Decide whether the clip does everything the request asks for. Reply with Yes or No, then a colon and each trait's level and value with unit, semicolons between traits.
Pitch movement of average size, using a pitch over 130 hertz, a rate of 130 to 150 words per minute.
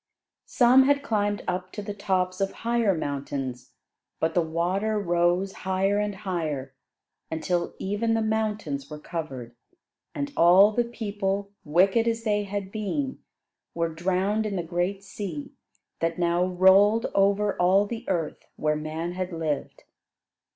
Yes: average, 3.7 semitones; high, 190 Hz; average, 145 wpm